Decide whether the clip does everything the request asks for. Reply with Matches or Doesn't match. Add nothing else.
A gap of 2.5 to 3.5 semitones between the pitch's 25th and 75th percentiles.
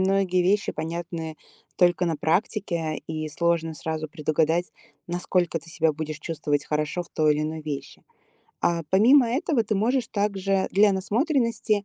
Doesn't match